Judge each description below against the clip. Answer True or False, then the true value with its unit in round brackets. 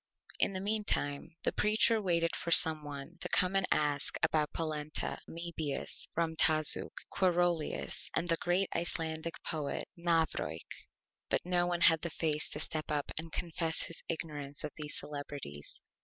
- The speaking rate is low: False (150 wpm)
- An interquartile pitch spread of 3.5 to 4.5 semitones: False (2.6 semitones)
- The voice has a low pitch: False (160 Hz)